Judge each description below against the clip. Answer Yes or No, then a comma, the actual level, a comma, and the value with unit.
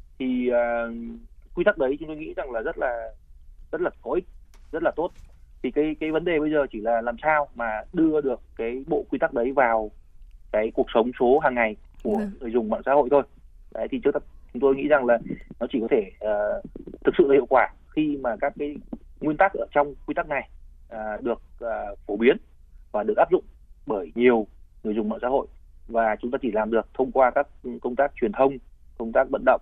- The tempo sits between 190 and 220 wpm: No, average, 230 wpm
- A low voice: Yes, low, 120 Hz